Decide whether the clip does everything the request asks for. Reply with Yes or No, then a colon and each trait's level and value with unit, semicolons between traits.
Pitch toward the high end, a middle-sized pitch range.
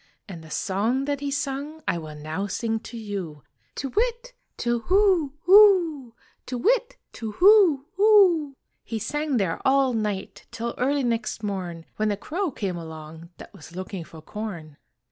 No: high, 235 Hz; wide, 8.1 semitones